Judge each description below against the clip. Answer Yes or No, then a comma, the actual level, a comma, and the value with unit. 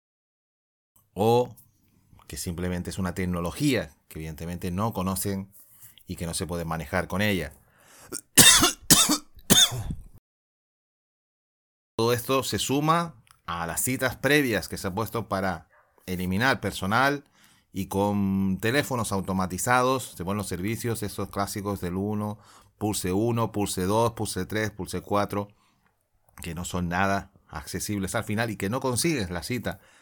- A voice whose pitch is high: No, low, 100 Hz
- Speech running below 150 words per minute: Yes, average, 130 wpm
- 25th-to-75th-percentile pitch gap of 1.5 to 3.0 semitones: No, average, 3.5 semitones